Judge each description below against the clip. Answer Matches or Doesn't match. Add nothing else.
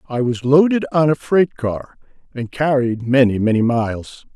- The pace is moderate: Matches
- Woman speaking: Doesn't match